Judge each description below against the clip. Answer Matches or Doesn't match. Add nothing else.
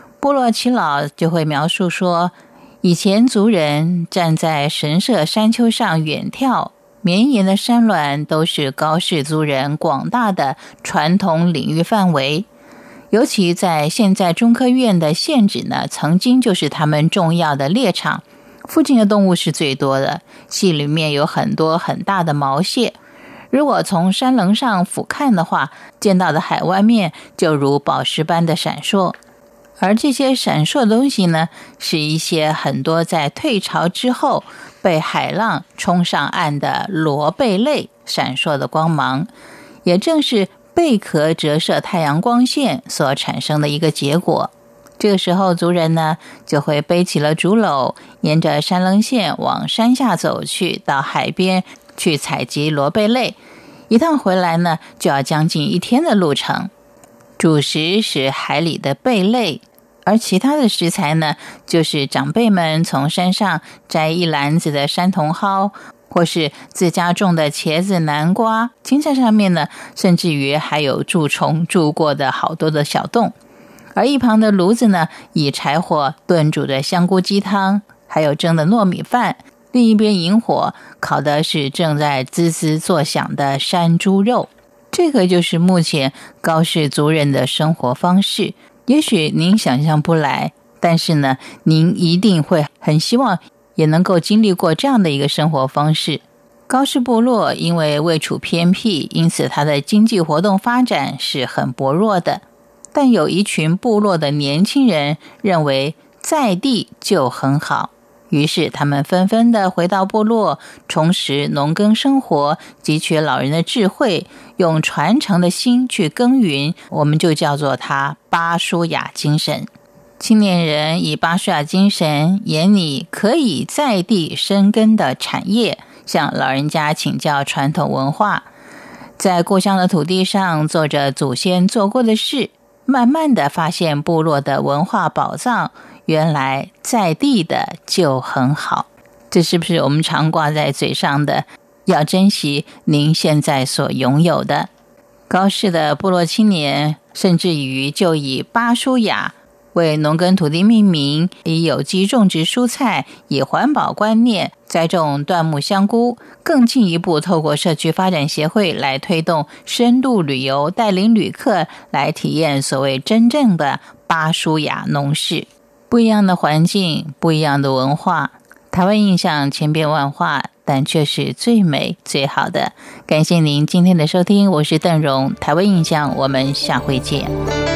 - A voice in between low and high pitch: Matches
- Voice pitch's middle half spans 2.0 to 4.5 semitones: Doesn't match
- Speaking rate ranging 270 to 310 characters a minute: Doesn't match